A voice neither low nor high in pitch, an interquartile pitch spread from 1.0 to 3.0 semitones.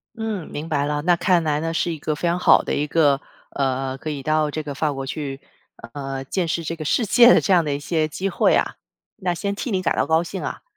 No: medium, 155 Hz; average, 3.4 semitones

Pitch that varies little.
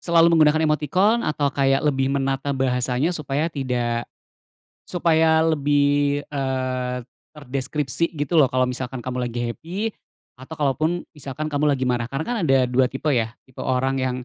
No: average, 3.0 semitones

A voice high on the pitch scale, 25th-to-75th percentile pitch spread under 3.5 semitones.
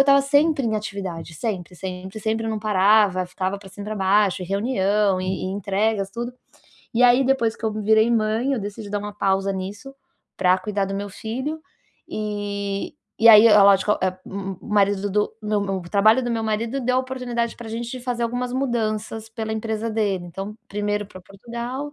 Yes: high, 210 Hz; average, 2.9 semitones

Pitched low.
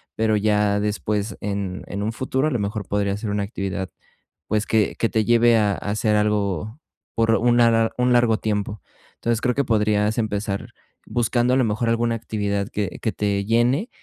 Yes: low, 110 Hz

